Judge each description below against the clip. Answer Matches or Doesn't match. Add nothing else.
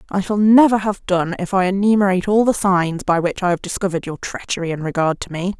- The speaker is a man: Doesn't match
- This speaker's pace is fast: Matches